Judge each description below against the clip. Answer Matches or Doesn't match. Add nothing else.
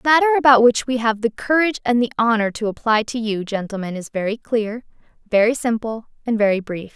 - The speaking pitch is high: Matches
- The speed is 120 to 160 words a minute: Doesn't match